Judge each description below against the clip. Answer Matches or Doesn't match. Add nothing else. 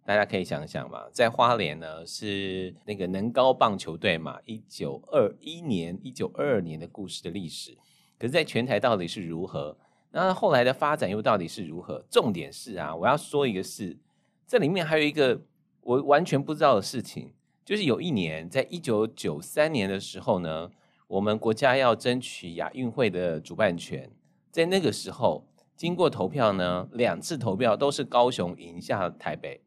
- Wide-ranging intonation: Matches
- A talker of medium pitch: Doesn't match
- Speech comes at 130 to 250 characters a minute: Doesn't match